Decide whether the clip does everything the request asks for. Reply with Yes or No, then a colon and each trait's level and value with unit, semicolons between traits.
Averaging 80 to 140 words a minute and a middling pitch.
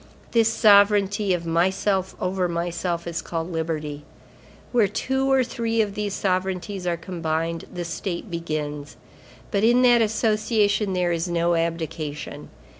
Yes: slow, 135 wpm; medium, 180 Hz